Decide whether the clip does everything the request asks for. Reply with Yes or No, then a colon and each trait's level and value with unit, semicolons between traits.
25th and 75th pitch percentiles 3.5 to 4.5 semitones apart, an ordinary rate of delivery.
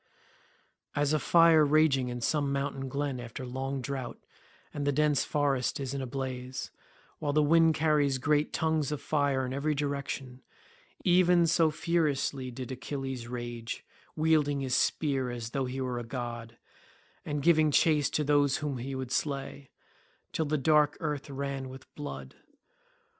No: narrow, 2.5 semitones; average, 155 wpm